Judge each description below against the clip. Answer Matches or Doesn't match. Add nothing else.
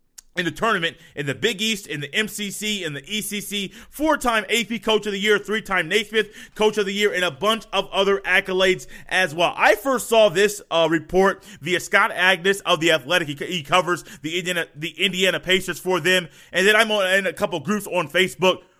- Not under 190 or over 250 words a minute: Matches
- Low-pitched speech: Doesn't match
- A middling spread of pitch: Matches